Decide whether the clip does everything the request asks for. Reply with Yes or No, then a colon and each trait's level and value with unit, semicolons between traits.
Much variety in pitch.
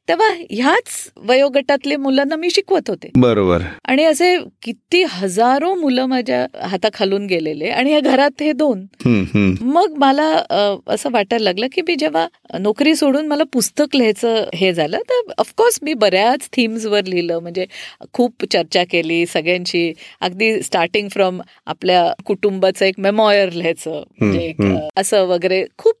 Yes: wide, 7.9 semitones